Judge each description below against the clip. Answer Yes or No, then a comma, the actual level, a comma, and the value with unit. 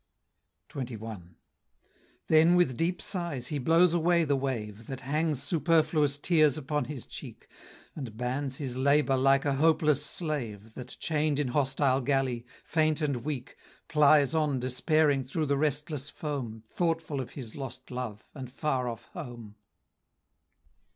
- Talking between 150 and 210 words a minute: No, average, 140 wpm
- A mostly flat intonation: No, average, 3.3 semitones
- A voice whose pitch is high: No, medium, 140 Hz